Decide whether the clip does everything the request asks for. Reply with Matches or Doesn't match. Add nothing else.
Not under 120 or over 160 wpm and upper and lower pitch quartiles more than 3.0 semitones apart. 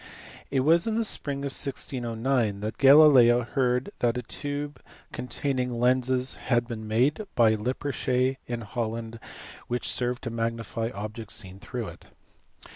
Doesn't match